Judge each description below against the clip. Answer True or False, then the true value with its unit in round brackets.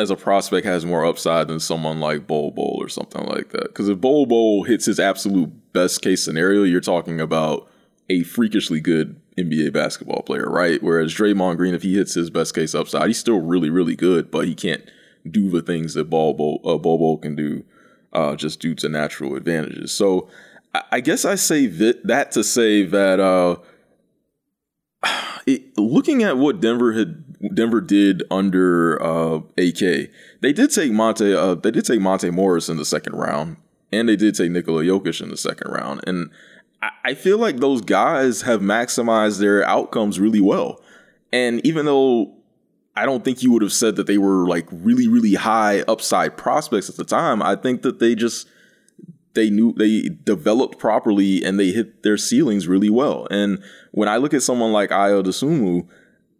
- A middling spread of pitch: True (4.6 semitones)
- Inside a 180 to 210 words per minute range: True (185 wpm)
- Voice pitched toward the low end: True (100 Hz)